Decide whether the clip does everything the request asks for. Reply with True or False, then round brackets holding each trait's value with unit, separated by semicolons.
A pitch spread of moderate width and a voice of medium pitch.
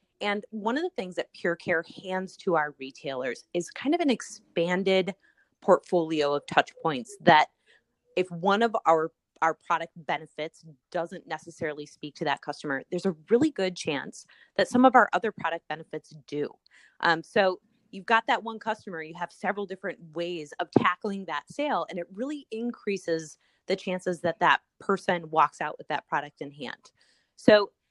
True (4.1 semitones; 180 Hz)